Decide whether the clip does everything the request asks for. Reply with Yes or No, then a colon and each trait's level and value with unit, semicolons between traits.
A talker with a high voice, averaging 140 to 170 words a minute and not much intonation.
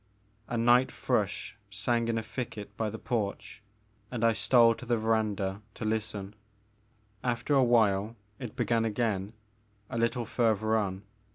No: low, 110 Hz; average, 150 wpm; narrow, 2.2 semitones